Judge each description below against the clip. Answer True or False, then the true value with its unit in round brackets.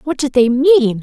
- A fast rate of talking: True (235 wpm)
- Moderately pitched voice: False (260 Hz)